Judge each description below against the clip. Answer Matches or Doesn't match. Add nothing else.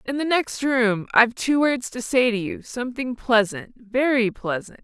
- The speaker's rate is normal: Matches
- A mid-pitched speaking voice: Doesn't match